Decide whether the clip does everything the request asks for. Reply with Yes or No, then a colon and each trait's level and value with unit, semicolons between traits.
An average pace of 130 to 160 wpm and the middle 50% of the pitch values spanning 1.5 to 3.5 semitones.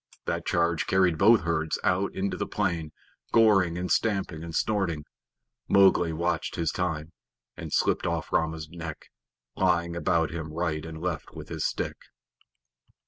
Yes: average, 145 wpm; narrow, 2.6 semitones